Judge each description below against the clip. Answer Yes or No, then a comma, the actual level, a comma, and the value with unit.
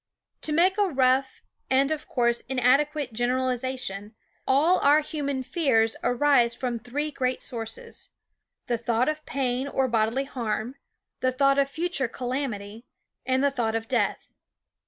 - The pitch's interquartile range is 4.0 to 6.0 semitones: No, average, 2.9 semitones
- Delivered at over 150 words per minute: No, average, 145 wpm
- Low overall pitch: No, very high, 260 Hz